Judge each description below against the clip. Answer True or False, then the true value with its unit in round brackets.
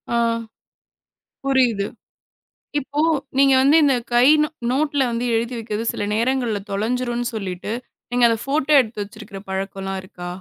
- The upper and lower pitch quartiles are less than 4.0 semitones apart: False (4.3 semitones)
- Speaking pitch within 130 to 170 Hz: False (235 Hz)